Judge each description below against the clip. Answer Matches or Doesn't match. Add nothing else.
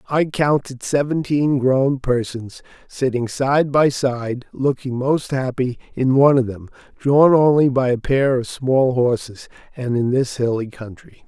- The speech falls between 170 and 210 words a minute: Doesn't match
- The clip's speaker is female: Doesn't match